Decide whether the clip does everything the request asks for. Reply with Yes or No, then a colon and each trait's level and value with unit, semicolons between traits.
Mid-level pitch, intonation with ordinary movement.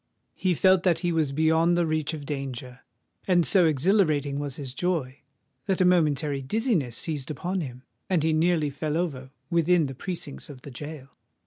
Yes: medium, 155 Hz; average, 4.0 semitones